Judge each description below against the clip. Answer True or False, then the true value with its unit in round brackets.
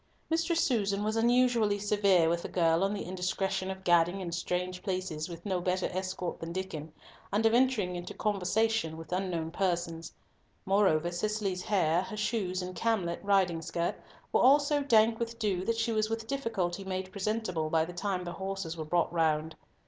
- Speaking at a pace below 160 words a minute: False (180 wpm)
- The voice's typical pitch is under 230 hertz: True (190 Hz)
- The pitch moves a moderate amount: True (3.7 semitones)